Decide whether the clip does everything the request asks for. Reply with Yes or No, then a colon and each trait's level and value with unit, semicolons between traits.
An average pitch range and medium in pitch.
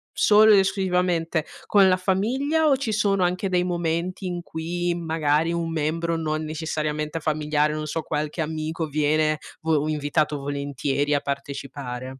Yes: average, 3.0 semitones; medium, 160 Hz